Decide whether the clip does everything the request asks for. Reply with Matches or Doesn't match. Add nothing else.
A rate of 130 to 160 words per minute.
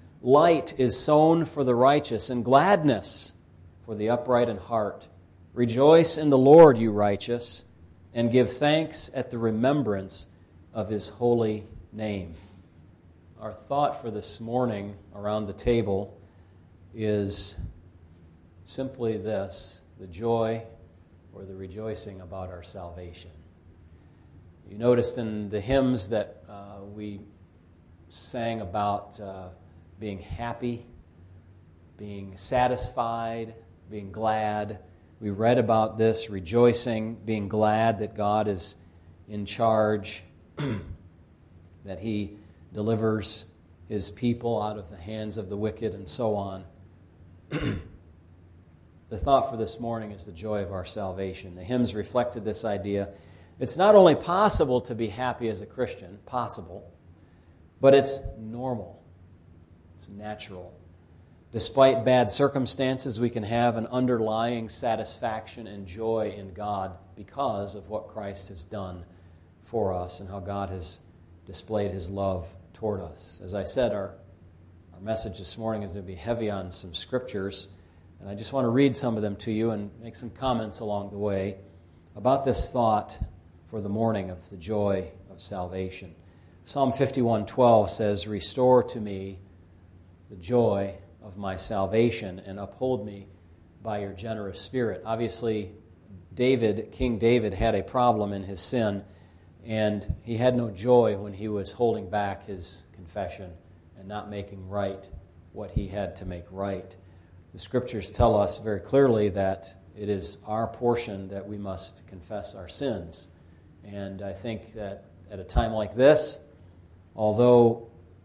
Matches